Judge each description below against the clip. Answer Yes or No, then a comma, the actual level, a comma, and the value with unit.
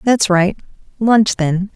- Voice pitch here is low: No, high, 200 Hz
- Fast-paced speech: No, slow, 135 wpm